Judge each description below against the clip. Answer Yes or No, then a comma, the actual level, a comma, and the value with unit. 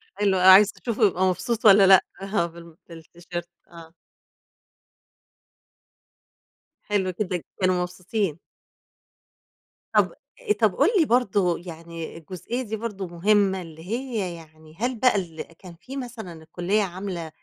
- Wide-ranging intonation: No, average, 3.6 semitones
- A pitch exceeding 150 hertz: Yes, medium, 185 Hz